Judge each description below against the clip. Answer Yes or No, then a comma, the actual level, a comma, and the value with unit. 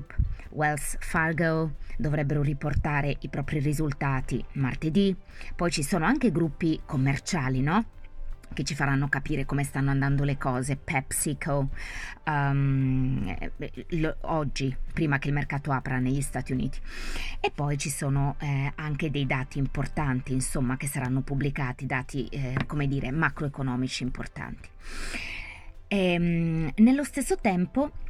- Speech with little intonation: No, average, 3.0 semitones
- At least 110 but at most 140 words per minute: Yes, average, 130 wpm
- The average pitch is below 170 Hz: Yes, medium, 140 Hz